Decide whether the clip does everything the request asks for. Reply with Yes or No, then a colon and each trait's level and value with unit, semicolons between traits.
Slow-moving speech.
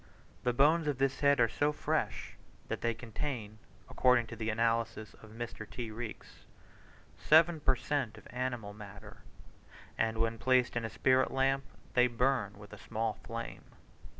No: average, 160 wpm